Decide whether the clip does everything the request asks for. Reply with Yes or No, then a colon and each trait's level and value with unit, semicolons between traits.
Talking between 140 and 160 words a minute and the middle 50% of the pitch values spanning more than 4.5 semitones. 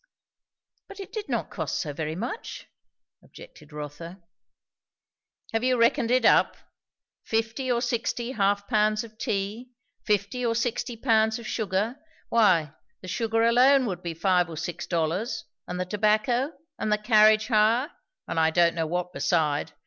Yes: average, 155 wpm; average, 5.0 semitones